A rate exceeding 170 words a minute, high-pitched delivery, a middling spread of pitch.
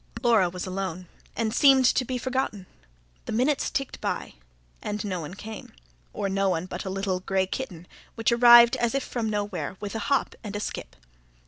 Yes: average, 190 wpm; high, 210 Hz; average, 4.0 semitones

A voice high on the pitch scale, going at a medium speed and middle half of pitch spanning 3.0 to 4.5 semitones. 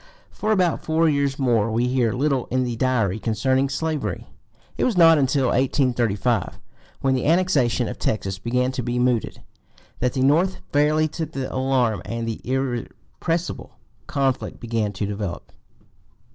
No: low, 130 Hz; average, 150 wpm; average, 3.8 semitones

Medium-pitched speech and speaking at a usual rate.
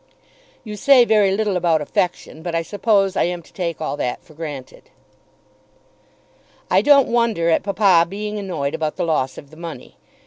Yes: medium, 180 Hz; average, 175 wpm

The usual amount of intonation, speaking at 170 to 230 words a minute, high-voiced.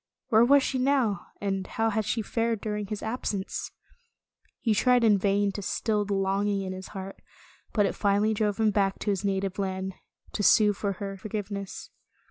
No: narrow, 2.0 semitones; average, 185 wpm; high, 205 Hz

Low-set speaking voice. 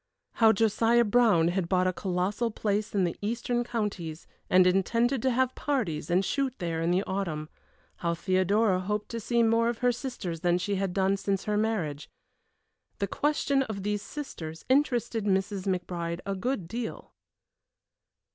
No: high, 200 Hz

